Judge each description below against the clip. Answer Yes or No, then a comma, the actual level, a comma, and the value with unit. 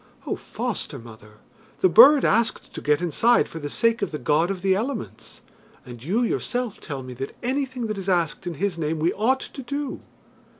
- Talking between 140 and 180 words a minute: No, average, 200 wpm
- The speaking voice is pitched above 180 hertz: Yes, high, 190 Hz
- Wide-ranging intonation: Yes, wide, 8.0 semitones